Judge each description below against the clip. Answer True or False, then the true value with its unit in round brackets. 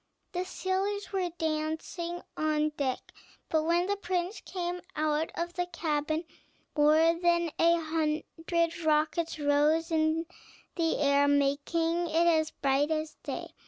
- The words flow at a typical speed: False (130 wpm)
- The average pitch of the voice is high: True (325 Hz)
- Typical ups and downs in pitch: False (2.0 semitones)